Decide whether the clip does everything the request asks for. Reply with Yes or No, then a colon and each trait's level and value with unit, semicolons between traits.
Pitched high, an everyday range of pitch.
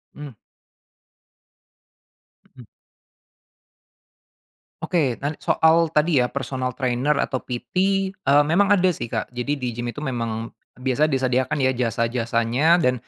No: low, 130 Hz; average, 3.5 semitones